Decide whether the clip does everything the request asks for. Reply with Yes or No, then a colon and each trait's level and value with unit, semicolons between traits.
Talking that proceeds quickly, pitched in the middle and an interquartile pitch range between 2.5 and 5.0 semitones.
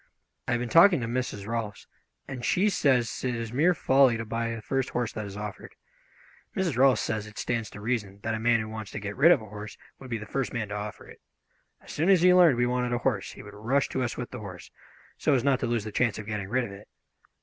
No: fast, 265 wpm; low, 115 Hz; average, 3.6 semitones